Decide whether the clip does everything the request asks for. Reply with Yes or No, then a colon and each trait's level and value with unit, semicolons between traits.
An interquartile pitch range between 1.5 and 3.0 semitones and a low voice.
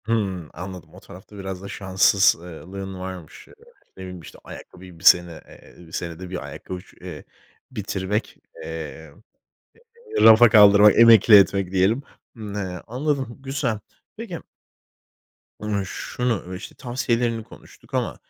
No: average, 3.5 semitones; very low, 95 Hz